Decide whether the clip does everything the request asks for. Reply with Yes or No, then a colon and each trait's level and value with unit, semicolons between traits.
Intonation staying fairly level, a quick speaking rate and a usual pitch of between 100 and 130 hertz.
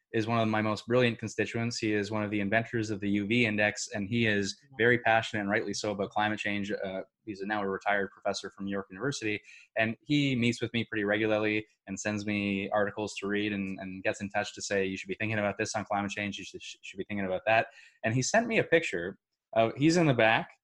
Yes: narrow, 1.9 semitones; fast, 245 wpm; low, 105 Hz